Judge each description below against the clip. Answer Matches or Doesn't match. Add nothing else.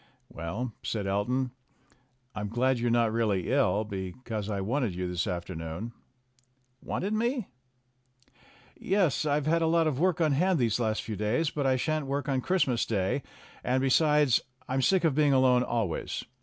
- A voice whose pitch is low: Matches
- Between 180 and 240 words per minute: Doesn't match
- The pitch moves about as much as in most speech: Doesn't match